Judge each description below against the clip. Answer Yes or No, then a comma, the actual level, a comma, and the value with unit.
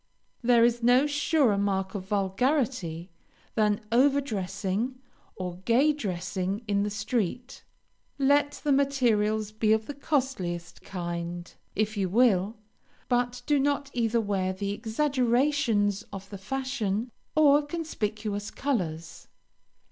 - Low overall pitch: No, high, 220 Hz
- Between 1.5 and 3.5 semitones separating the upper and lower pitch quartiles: No, wide, 5.4 semitones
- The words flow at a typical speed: No, slow, 120 wpm